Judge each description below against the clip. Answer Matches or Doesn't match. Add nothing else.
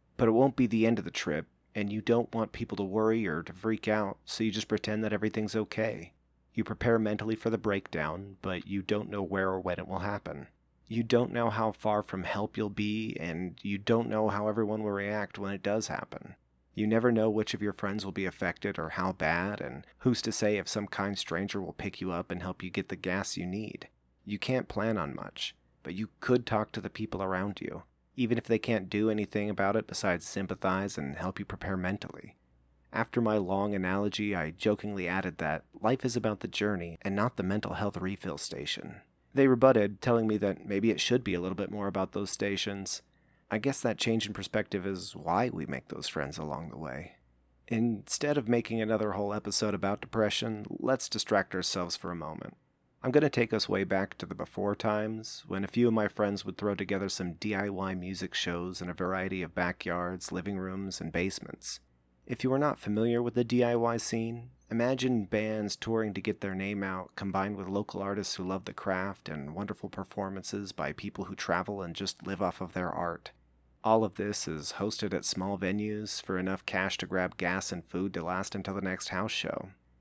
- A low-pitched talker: Matches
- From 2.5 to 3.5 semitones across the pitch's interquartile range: Matches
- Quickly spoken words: Matches